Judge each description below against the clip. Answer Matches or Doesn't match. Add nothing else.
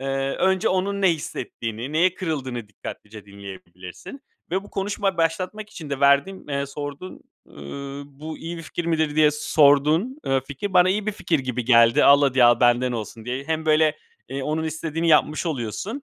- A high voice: Doesn't match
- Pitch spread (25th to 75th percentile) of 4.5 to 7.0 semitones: Matches